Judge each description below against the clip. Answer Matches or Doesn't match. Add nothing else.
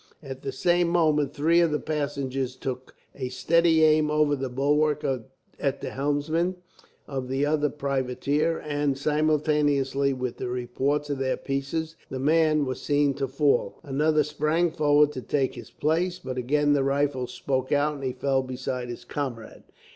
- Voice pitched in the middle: Matches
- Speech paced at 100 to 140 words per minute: Doesn't match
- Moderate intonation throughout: Doesn't match